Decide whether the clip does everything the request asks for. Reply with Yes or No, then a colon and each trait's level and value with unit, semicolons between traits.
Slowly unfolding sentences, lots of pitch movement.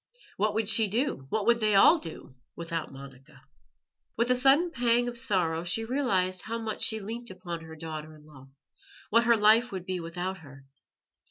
No: average, 185 wpm; wide, 6.2 semitones